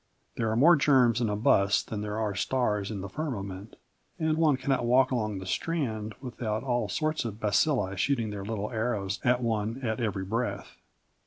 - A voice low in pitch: Yes, low, 110 Hz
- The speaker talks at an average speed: Yes, average, 185 wpm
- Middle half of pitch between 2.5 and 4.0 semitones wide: Yes, average, 3.7 semitones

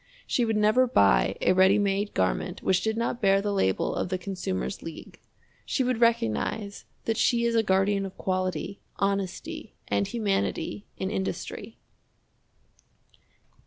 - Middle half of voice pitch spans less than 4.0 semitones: Yes, average, 2.9 semitones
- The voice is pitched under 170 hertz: No, high, 195 Hz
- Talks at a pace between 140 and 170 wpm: Yes, average, 145 wpm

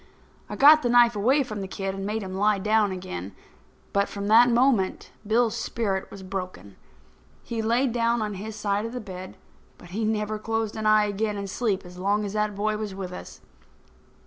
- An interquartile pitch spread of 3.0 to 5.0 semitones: No, narrow, 2.5 semitones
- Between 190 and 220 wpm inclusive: Yes, average, 200 wpm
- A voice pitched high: Yes, high, 210 Hz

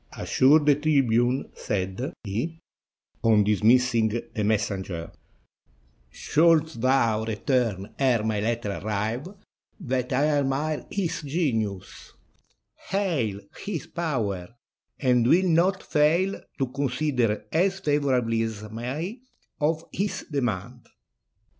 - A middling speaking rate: No, slow, 105 wpm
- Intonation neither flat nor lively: No, wide, 5.7 semitones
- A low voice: Yes, low, 125 Hz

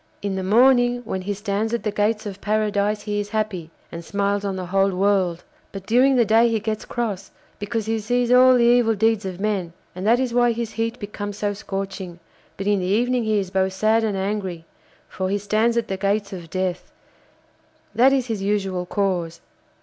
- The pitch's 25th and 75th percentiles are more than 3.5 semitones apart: No, average, 2.7 semitones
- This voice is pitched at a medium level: No, high, 205 Hz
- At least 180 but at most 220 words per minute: Yes, fast, 205 wpm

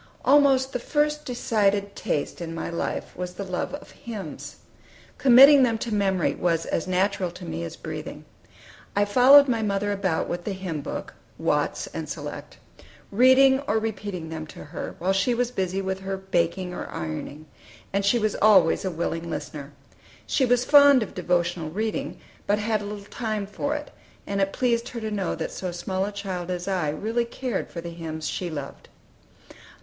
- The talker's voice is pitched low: No, high, 200 Hz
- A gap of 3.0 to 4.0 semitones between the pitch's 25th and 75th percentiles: No, average, 4.9 semitones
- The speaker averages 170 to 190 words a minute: Yes, average, 180 wpm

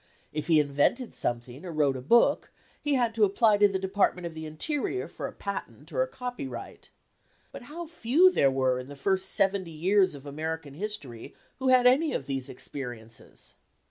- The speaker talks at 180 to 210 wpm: Yes, average, 185 wpm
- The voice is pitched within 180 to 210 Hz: Yes, medium, 185 Hz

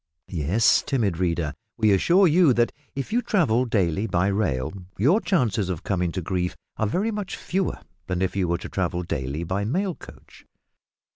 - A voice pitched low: Yes, low, 100 Hz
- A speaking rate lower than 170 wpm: No, average, 180 wpm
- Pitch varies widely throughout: Yes, wide, 8.4 semitones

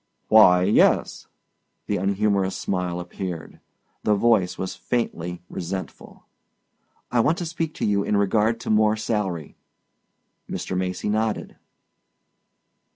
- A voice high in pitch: No, low, 100 Hz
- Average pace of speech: No, slow, 115 wpm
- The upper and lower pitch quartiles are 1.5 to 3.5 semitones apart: Yes, average, 3.1 semitones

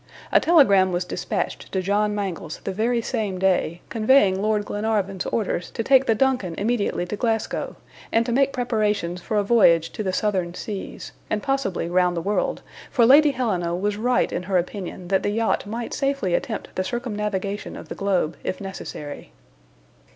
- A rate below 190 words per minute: Yes, average, 175 wpm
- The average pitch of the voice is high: Yes, high, 205 Hz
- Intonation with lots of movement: No, average, 3.7 semitones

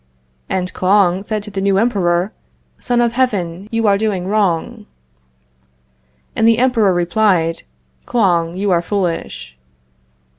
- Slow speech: Yes, slow, 125 wpm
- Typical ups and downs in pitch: Yes, average, 3.6 semitones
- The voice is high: Yes, high, 200 Hz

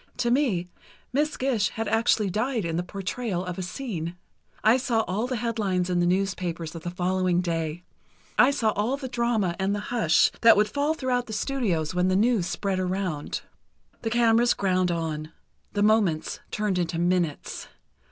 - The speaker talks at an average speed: Yes, average, 170 wpm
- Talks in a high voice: Yes, high, 195 Hz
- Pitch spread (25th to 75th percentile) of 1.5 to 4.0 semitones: No, average, 4.8 semitones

